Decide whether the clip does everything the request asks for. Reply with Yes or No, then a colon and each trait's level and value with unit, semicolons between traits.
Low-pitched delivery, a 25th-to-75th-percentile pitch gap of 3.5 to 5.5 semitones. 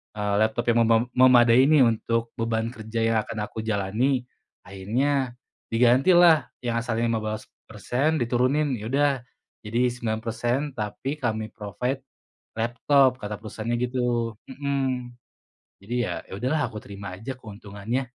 No: low, 120 Hz; average, 3.0 semitones